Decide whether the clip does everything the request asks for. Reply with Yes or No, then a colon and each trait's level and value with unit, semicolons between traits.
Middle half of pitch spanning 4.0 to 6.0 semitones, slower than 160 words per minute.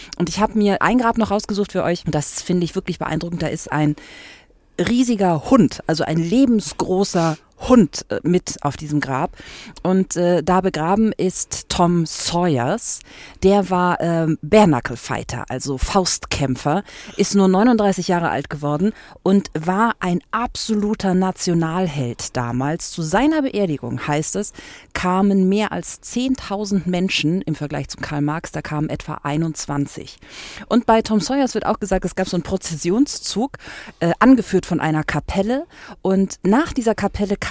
Yes: average, 4.6 semitones; average, 150 wpm